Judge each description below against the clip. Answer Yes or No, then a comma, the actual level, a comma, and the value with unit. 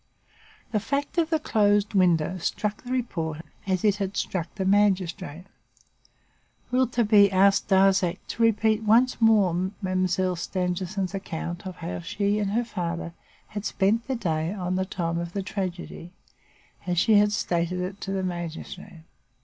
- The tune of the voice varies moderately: Yes, average, 3.0 semitones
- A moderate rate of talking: Yes, average, 150 wpm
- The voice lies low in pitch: No, high, 190 Hz